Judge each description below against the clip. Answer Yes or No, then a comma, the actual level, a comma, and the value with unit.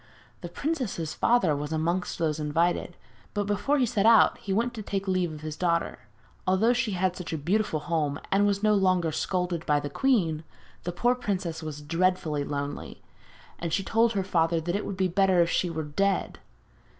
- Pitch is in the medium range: Yes, medium, 180 Hz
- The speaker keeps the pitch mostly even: No, average, 4.1 semitones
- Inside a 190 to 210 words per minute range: Yes, average, 195 wpm